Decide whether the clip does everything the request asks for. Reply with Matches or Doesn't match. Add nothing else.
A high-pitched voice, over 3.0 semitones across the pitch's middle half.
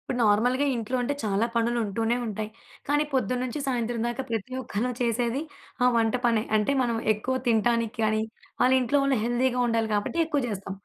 Doesn't match